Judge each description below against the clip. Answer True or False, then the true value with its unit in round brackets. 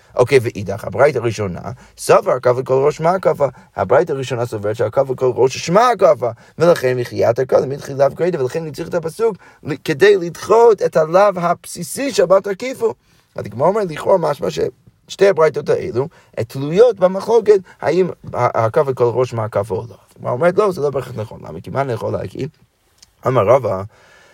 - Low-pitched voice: False (155 Hz)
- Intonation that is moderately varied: False (7.4 semitones)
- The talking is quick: True (170 wpm)